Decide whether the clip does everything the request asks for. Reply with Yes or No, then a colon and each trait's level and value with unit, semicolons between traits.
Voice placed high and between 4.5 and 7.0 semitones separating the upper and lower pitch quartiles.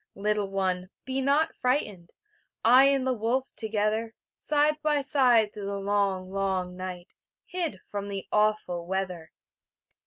Yes: high, 210 Hz; average, 5.3 semitones